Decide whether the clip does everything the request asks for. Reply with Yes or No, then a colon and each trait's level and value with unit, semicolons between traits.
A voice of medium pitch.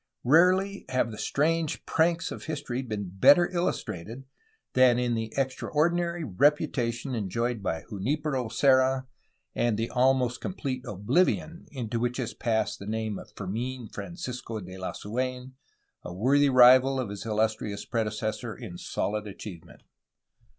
No: low, 125 Hz